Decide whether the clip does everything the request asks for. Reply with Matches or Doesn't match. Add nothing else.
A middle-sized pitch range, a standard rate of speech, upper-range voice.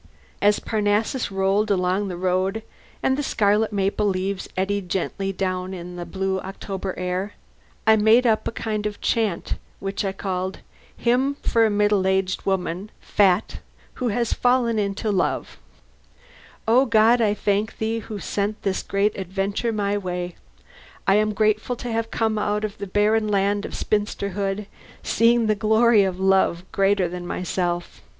Doesn't match